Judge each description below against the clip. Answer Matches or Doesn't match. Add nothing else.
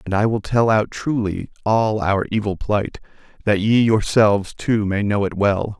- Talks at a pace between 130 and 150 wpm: Doesn't match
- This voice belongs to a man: Matches